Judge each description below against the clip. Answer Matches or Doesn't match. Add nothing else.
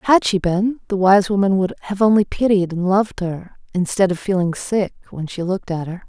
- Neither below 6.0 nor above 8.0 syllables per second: Doesn't match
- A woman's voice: Matches